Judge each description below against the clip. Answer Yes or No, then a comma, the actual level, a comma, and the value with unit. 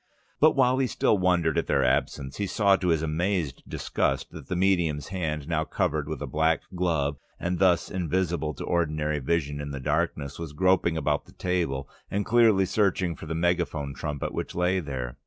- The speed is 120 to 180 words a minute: No, average, 195 wpm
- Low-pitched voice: Yes, very low, 85 Hz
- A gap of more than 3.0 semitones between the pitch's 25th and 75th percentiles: Yes, average, 3.9 semitones